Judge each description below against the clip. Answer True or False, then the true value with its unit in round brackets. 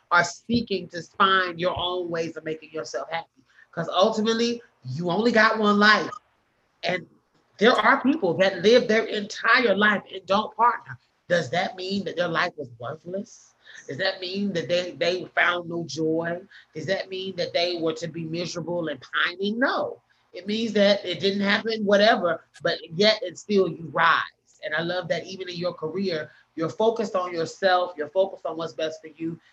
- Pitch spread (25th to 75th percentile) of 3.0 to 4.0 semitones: True (3.4 semitones)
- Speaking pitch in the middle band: True (180 Hz)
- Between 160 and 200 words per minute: True (185 wpm)